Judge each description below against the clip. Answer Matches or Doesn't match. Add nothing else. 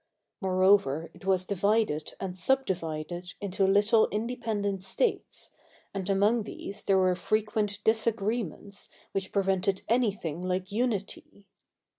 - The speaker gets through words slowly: Matches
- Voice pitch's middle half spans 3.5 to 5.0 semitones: Doesn't match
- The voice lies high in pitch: Matches